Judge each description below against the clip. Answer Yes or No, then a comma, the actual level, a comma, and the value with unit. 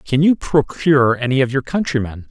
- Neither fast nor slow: Yes, average, 180 wpm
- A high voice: No, low, 135 Hz